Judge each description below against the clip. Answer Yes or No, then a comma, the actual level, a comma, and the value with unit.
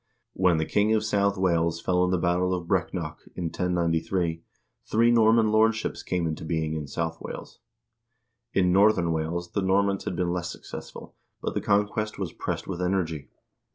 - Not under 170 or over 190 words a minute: Yes, average, 175 wpm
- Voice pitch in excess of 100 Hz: No, very low, 90 Hz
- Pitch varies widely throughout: No, average, 3.2 semitones